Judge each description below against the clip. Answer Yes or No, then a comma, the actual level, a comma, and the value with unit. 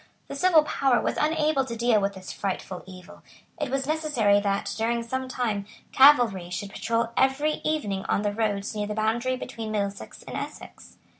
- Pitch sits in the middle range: No, high, 230 Hz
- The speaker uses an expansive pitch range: No, average, 4.9 semitones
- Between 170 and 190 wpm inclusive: Yes, average, 175 wpm